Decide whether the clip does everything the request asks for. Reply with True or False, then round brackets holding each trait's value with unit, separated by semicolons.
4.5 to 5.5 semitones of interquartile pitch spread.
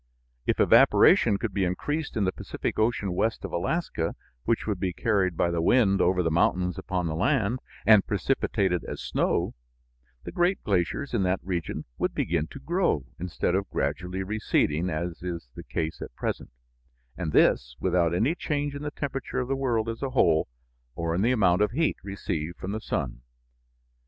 True (5.2 semitones)